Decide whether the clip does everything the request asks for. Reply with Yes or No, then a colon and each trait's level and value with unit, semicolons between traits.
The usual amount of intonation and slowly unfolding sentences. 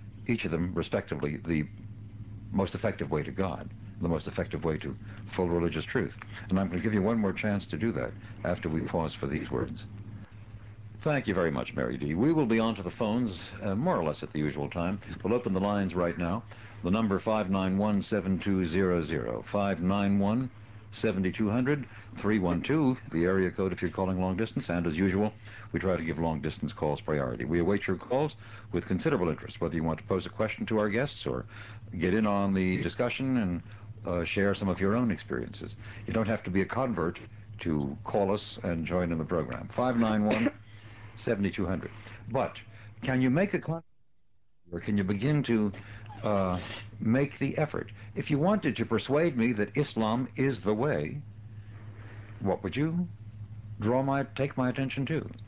No: average, 3.1 semitones; average, 180 wpm